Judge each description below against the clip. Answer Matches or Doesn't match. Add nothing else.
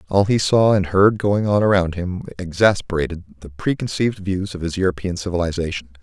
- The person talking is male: Matches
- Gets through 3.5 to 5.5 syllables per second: Doesn't match